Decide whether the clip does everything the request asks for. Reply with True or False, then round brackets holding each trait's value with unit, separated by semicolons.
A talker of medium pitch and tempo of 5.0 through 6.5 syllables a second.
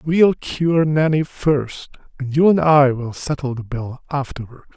False (145 Hz; 4.0 syllables/s)